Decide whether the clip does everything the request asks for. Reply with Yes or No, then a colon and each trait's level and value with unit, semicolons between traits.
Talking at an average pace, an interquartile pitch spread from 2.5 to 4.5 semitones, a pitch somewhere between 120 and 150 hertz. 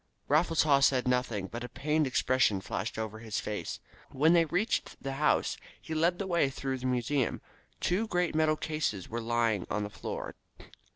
No: average, 180 wpm; wide, 5.4 semitones; low, 135 Hz